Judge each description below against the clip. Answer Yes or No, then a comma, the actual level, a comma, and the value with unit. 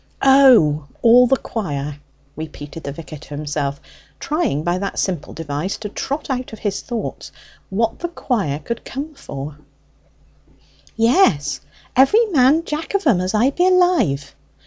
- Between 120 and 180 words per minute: Yes, average, 145 wpm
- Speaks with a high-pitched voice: Yes, high, 210 Hz